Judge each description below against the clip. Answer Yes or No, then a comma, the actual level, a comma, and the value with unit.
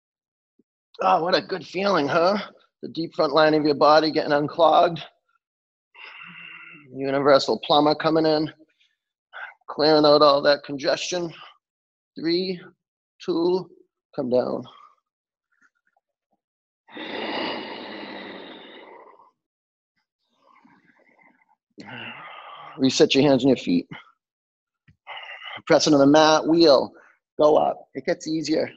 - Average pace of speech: No, slow, 90 wpm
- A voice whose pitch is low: No, medium, 170 Hz